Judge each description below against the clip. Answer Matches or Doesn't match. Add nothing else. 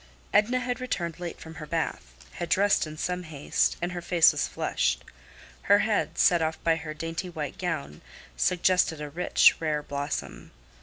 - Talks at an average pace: Matches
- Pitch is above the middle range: Doesn't match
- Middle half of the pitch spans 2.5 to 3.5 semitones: Matches